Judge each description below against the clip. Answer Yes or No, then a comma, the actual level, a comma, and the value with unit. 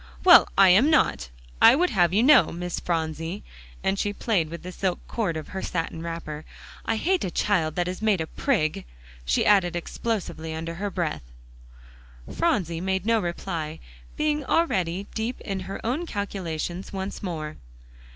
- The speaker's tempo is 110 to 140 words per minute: No, average, 165 wpm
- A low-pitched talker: No, medium, 185 Hz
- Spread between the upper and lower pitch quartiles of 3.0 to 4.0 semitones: No, average, 4.6 semitones